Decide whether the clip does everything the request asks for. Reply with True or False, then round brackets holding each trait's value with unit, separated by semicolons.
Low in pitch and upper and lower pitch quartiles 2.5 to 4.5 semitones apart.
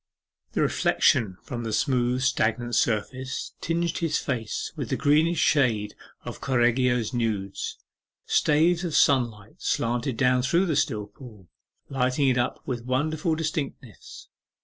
True (125 Hz; 4.1 semitones)